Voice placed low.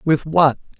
No: medium, 155 Hz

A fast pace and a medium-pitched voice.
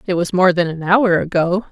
Yes: fast, 245 wpm; medium, 180 Hz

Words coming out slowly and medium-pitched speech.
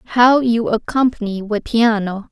No: slow, 130 wpm; high, 225 Hz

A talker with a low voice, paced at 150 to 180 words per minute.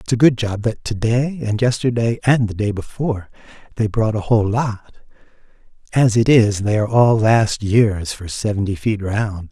No: low, 110 Hz; average, 190 wpm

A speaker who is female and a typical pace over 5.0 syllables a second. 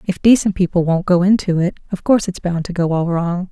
Yes: female; 5.9 syllables/s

